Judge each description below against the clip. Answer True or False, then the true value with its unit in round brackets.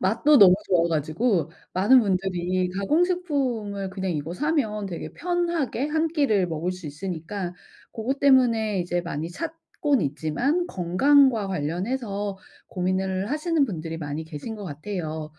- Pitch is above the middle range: True (195 Hz)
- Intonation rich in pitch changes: True (7.4 semitones)